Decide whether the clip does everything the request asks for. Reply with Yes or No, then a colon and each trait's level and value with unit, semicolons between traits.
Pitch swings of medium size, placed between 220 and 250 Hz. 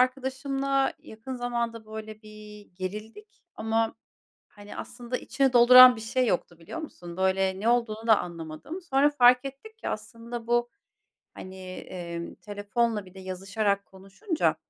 Yes: average, 4.4 semitones; high, 225 Hz